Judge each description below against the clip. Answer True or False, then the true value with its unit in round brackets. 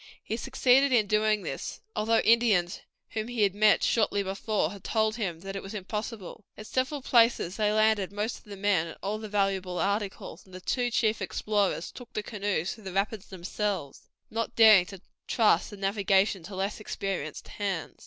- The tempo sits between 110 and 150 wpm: False (185 wpm)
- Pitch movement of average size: False (2.2 semitones)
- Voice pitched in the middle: False (205 Hz)